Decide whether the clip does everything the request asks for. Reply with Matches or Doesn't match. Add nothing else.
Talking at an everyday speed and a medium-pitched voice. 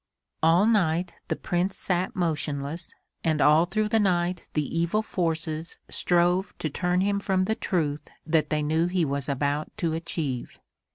Matches